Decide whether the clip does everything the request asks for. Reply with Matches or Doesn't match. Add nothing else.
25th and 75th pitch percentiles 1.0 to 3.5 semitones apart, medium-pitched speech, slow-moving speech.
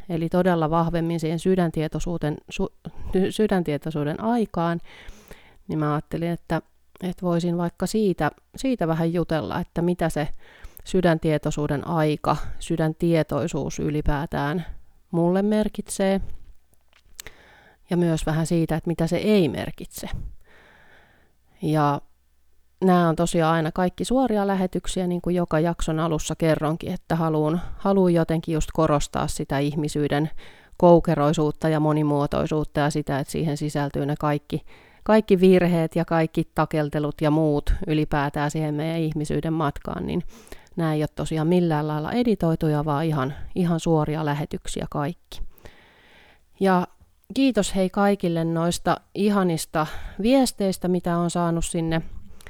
Doesn't match